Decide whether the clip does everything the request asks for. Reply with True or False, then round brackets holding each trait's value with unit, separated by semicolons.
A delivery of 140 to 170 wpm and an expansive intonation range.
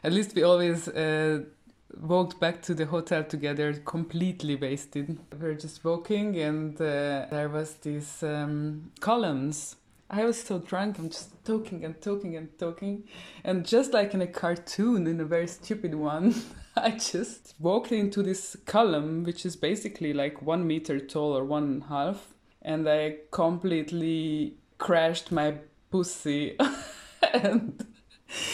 False (150 wpm; 3.9 semitones)